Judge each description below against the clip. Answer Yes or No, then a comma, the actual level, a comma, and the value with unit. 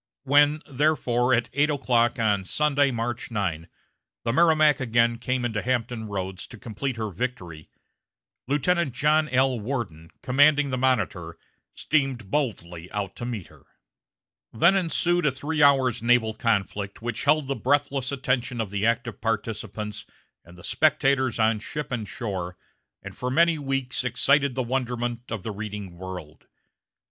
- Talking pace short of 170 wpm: Yes, average, 150 wpm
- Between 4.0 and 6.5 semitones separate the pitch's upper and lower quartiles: Yes, average, 4.5 semitones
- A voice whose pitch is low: Yes, low, 120 Hz